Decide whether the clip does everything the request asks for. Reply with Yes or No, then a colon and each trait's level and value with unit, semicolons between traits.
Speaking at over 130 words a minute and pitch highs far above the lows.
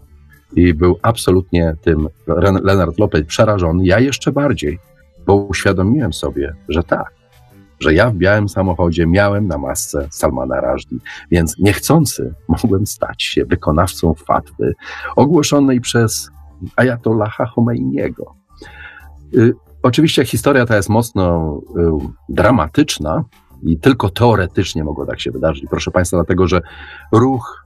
No: average, 125 wpm; wide, 5.7 semitones